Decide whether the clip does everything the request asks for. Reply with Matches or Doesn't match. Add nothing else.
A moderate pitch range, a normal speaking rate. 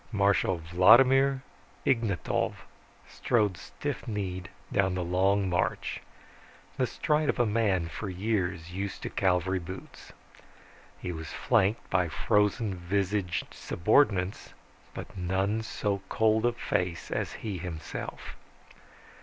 Doesn't match